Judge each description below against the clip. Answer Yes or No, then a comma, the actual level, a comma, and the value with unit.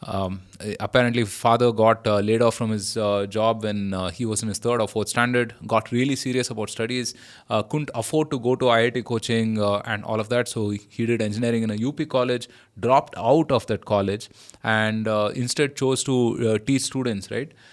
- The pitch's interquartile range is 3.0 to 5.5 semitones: No, narrow, 2.6 semitones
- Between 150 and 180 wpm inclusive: No, fast, 205 wpm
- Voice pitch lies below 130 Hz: Yes, low, 115 Hz